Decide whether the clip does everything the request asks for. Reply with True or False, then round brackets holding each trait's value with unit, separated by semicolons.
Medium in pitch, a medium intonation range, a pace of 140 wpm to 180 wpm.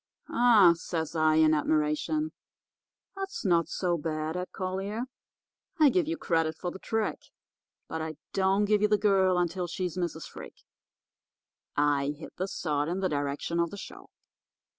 True (175 Hz; 4.0 semitones; 160 wpm)